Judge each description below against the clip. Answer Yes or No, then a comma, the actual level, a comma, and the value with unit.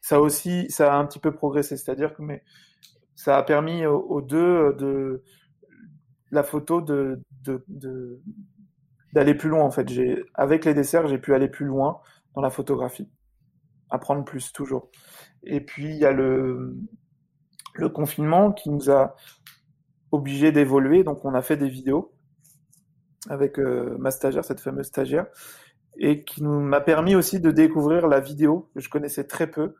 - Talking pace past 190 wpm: No, average, 165 wpm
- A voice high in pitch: No, medium, 145 Hz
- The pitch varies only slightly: Yes, narrow, 2.1 semitones